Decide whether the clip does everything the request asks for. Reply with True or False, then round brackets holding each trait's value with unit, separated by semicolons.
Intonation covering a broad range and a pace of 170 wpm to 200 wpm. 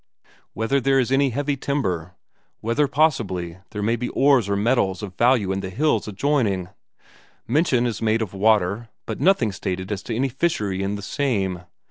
True (5.8 semitones; 175 wpm)